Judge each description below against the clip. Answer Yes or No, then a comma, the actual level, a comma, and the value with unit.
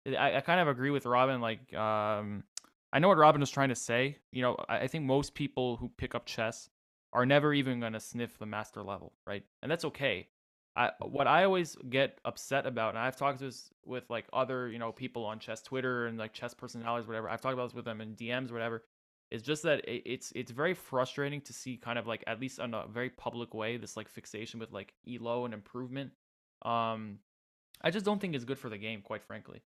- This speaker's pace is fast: Yes, fast, 230 wpm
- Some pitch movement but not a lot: Yes, average, 3.1 semitones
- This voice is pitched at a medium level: No, low, 120 Hz